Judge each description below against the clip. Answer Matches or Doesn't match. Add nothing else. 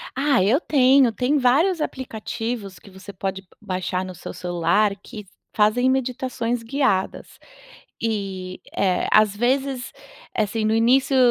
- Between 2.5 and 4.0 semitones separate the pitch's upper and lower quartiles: Doesn't match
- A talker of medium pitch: Doesn't match